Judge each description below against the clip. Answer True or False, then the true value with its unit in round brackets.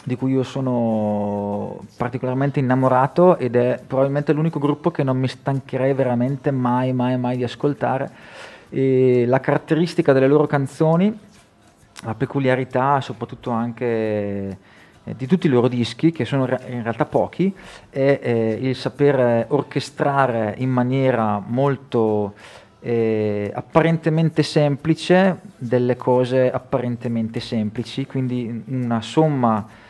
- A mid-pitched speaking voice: False (130 Hz)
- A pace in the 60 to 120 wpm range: True (115 wpm)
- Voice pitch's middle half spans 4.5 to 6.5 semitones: False (3.2 semitones)